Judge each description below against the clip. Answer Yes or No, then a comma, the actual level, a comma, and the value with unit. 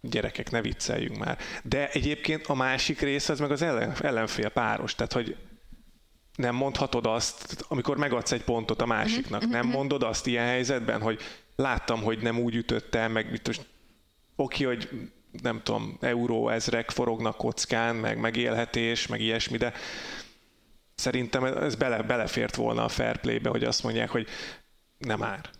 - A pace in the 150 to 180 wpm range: Yes, fast, 155 wpm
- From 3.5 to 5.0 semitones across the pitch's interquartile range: No, average, 3.0 semitones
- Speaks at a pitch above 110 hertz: Yes, low, 120 Hz